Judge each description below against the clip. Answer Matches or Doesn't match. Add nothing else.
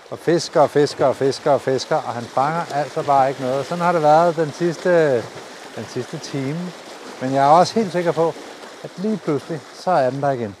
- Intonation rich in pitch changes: Doesn't match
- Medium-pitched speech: Matches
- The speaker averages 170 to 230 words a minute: Matches